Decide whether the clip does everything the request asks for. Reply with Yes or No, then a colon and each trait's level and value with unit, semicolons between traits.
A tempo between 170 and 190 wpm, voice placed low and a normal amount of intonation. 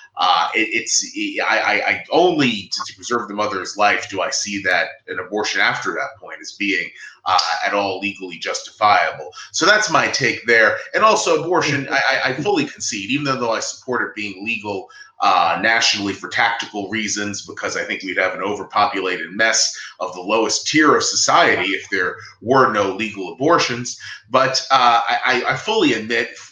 No: average, 175 wpm; low, 110 Hz; wide, 8.8 semitones